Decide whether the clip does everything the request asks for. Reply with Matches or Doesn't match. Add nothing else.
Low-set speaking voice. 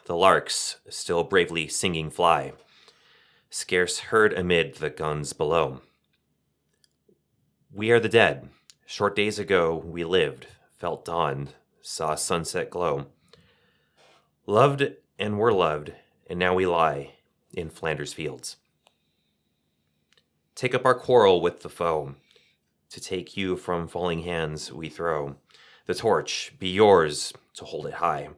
Matches